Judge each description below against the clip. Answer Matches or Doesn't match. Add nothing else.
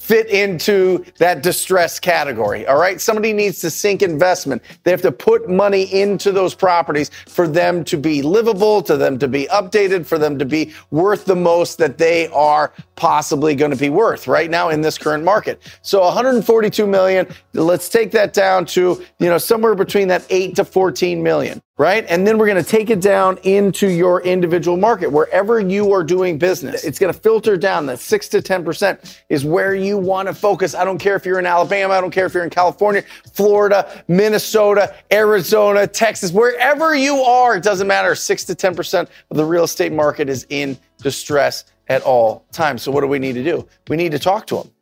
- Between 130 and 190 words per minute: Doesn't match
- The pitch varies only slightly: Doesn't match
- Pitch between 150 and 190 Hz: Matches